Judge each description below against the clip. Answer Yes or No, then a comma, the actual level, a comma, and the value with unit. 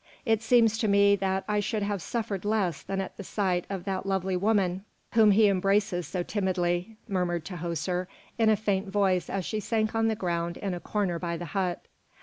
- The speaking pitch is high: Yes, high, 195 Hz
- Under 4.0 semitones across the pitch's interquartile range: Yes, average, 2.8 semitones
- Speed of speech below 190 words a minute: No, average, 200 wpm